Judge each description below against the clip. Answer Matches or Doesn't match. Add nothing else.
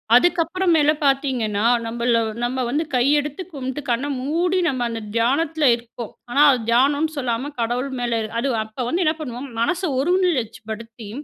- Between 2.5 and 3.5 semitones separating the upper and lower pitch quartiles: Doesn't match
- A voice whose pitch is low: Doesn't match